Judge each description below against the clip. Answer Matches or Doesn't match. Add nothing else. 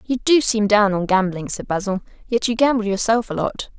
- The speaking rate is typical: Doesn't match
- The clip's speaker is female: Matches